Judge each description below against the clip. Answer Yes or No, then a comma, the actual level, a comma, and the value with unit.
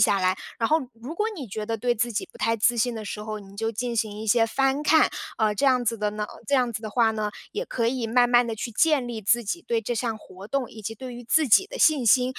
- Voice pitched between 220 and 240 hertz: Yes, high, 230 Hz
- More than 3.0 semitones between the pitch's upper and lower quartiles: No, average, 2.7 semitones